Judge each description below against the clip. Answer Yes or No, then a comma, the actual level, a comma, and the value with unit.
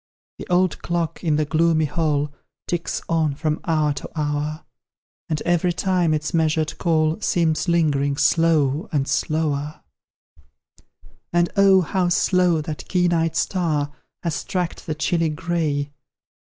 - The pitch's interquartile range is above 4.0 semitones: No, narrow, 2.4 semitones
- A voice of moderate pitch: Yes, medium, 160 Hz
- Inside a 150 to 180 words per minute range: No, slow, 135 wpm